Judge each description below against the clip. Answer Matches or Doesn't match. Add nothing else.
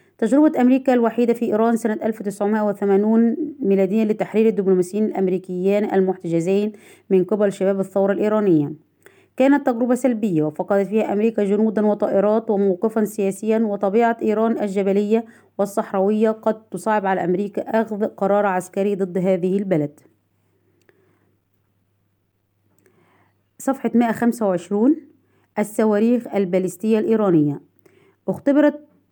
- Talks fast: Doesn't match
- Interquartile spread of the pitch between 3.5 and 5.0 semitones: Doesn't match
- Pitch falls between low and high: Doesn't match